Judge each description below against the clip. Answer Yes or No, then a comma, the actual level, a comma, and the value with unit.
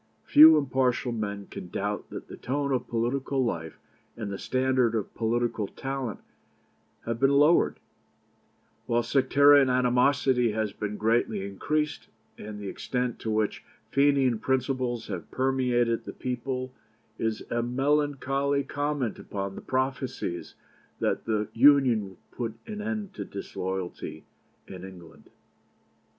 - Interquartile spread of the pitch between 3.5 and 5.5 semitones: Yes, average, 4.0 semitones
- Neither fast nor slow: No, slow, 130 wpm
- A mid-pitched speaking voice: No, low, 125 Hz